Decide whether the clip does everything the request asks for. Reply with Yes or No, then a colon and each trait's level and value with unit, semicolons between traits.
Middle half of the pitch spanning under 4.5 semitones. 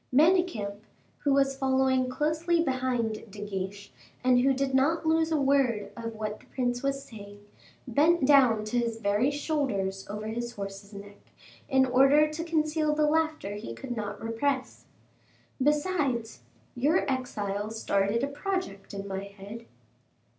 No: wide, 5.6 semitones